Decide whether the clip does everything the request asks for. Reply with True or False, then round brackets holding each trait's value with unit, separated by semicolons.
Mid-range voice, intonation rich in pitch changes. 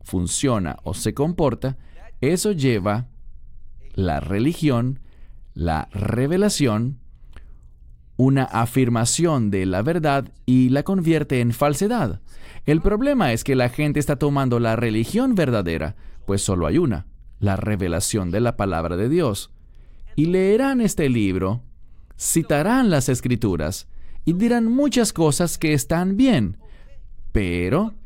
False (120 Hz; 8.4 semitones)